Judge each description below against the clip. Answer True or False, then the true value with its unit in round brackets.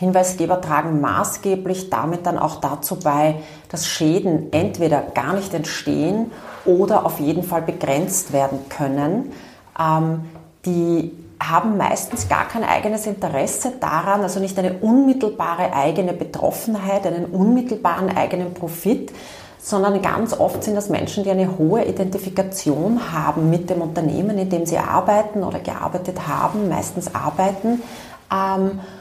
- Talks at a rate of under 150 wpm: True (130 wpm)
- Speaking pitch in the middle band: True (180 Hz)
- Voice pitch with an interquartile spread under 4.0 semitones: True (3.6 semitones)